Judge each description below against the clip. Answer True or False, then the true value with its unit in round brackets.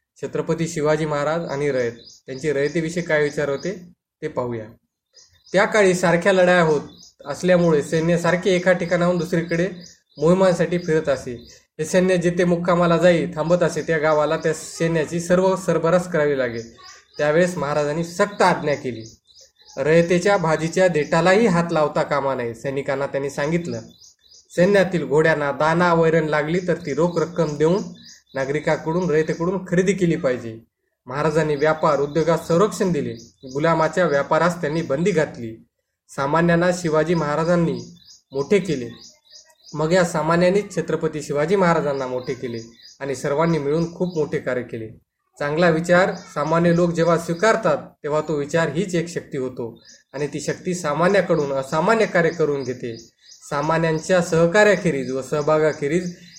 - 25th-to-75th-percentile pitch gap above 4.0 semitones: False (3.3 semitones)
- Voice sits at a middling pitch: True (160 Hz)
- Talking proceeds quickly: True (135 wpm)